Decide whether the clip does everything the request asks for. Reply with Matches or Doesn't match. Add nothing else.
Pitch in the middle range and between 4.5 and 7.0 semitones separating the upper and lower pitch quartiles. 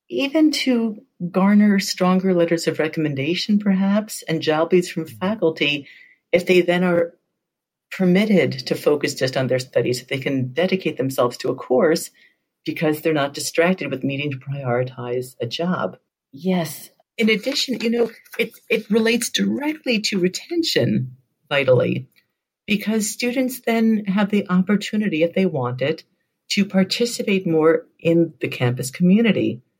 Matches